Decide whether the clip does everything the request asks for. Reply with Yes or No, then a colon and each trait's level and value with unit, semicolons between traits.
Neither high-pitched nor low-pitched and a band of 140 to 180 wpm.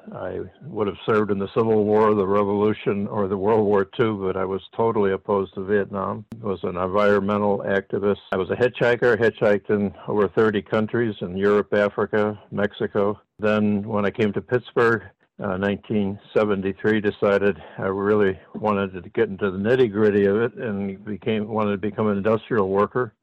No: low, 105 Hz; average, 175 wpm